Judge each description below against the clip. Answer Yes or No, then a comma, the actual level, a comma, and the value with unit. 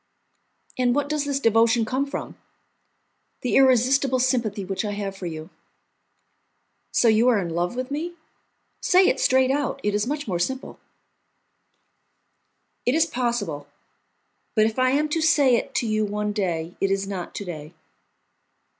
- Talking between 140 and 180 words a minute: Yes, average, 160 wpm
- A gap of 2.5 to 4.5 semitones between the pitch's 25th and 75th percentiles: No, average, 5.1 semitones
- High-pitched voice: Yes, high, 235 Hz